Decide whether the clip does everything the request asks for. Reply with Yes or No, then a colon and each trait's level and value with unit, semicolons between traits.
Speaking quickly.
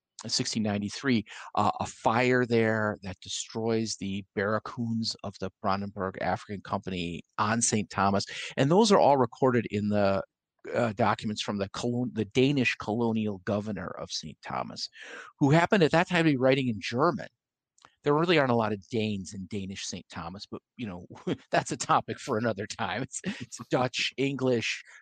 No: average, 170 wpm